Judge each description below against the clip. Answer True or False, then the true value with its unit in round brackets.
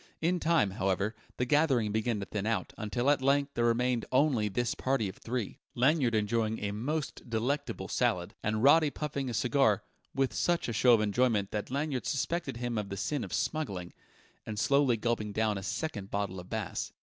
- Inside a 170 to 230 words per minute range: True (190 wpm)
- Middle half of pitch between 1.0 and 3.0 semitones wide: False (4.8 semitones)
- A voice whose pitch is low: True (120 Hz)